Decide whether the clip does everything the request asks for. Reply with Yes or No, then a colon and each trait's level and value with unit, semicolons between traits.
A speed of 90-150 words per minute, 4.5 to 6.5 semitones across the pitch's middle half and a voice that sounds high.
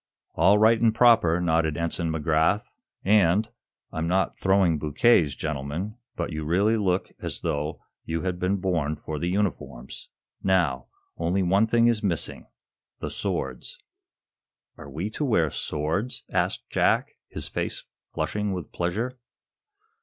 No: average, 140 wpm; average, 4.8 semitones; very low, 90 Hz